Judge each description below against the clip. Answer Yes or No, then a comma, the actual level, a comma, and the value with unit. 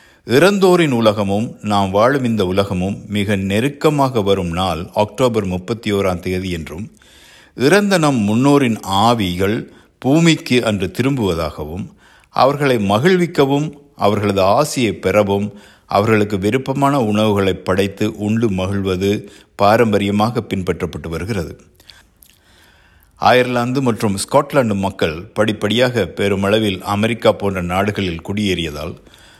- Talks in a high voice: No, low, 105 Hz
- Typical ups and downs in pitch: Yes, average, 3.9 semitones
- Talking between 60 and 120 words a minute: Yes, average, 90 wpm